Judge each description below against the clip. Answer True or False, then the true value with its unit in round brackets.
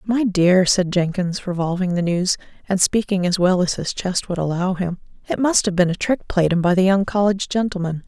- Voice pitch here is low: False (185 Hz)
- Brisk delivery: True (225 wpm)